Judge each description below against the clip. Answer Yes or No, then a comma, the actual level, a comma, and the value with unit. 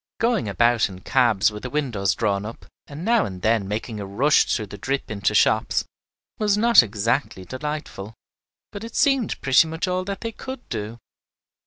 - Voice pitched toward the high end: No, low, 120 Hz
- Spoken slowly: No, average, 180 wpm